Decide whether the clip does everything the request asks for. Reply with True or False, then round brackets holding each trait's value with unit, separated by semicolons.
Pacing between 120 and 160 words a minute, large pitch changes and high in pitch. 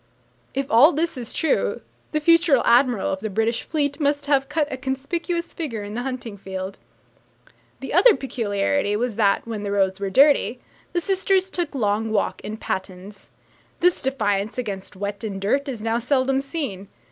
False (170 wpm; 5.9 semitones; 245 Hz)